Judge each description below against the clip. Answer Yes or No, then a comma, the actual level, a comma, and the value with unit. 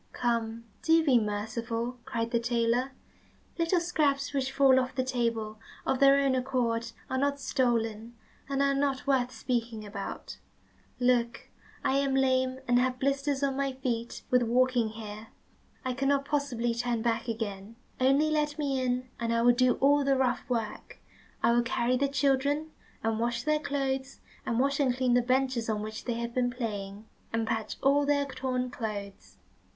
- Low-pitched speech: No, very high, 255 Hz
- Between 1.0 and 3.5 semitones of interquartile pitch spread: Yes, average, 2.9 semitones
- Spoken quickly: No, average, 170 wpm